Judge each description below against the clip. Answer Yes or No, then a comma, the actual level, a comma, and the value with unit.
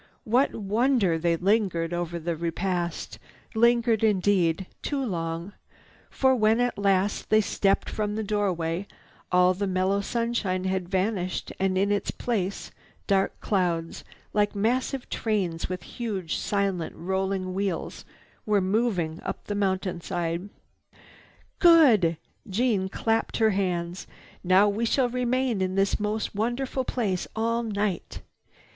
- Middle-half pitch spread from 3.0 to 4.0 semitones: Yes, average, 3.4 semitones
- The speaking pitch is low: No, high, 200 Hz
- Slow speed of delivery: Yes, slow, 125 wpm